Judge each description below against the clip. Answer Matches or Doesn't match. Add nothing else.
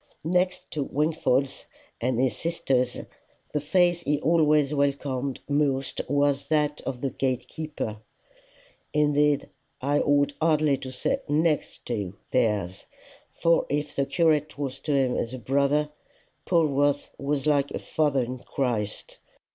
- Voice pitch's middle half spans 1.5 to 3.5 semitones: Matches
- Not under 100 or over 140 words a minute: Matches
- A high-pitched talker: Doesn't match